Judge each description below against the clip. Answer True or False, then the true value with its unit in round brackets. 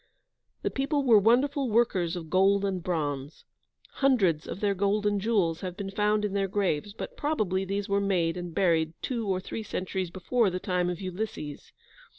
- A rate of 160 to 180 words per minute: True (175 wpm)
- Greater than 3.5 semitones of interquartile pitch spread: False (3.0 semitones)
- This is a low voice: False (195 Hz)